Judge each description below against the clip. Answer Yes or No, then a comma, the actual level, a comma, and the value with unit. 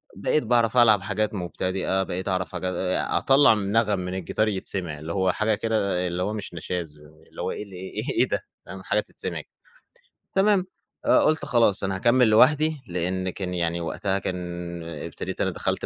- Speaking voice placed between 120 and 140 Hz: No, very low, 95 Hz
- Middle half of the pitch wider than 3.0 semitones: Yes, average, 3.4 semitones